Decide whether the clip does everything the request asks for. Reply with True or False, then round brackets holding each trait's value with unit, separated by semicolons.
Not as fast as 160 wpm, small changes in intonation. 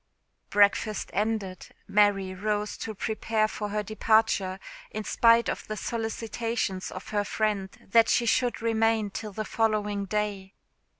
True (135 wpm; 1.7 semitones)